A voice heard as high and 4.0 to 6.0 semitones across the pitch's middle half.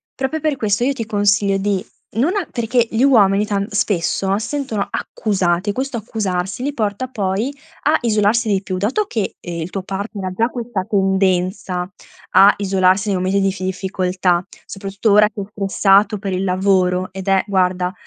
No: high, 200 Hz; average, 2.8 semitones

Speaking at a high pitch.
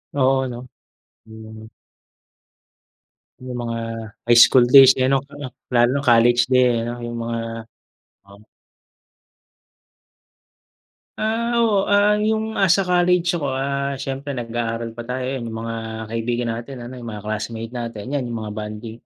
No: low, 120 Hz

